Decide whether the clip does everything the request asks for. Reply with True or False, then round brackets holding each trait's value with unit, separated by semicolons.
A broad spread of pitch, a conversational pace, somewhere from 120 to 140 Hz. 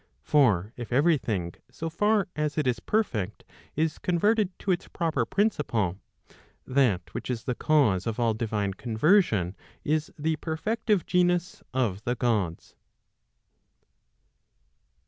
False (7.7 semitones; 125 wpm; 135 Hz)